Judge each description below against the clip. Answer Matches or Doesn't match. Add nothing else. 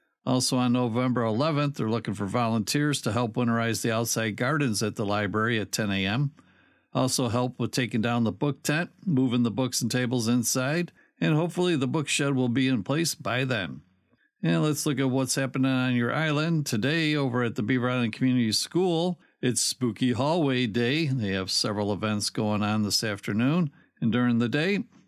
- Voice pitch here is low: Matches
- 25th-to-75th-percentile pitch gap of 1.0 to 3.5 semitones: Doesn't match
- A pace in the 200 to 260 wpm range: Doesn't match